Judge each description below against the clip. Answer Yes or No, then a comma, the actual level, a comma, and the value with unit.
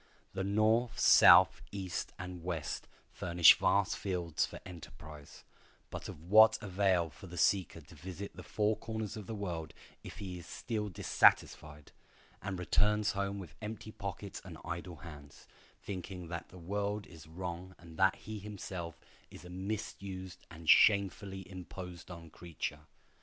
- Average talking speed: Yes, average, 150 wpm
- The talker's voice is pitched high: No, very low, 95 Hz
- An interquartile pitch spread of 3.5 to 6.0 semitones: No, average, 3.0 semitones